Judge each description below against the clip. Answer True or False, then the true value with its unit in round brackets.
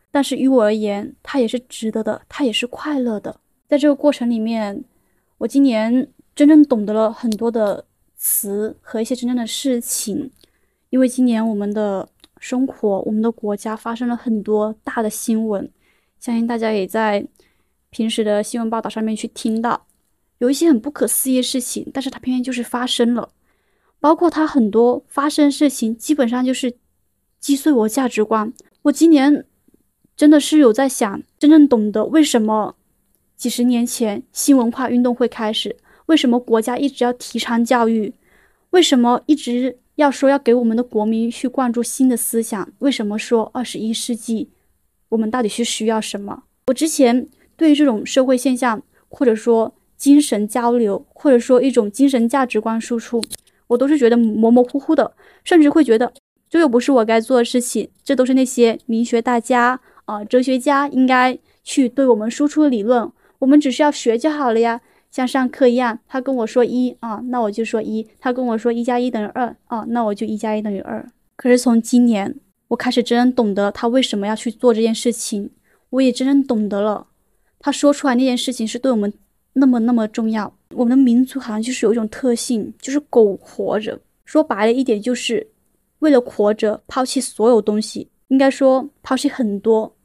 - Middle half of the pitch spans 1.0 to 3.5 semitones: True (2.8 semitones)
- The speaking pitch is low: False (245 Hz)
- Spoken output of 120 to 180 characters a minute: False (280 characters per minute)